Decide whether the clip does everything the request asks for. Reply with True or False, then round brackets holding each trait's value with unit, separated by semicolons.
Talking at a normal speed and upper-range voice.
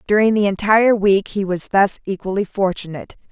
True (165 wpm; 200 Hz)